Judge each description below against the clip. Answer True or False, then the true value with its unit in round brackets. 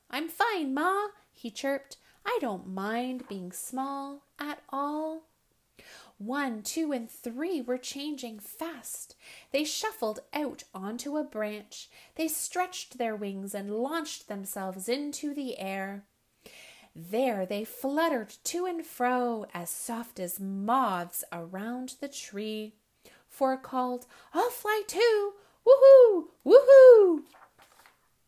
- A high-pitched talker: True (265 Hz)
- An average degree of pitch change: False (6.9 semitones)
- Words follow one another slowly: True (115 wpm)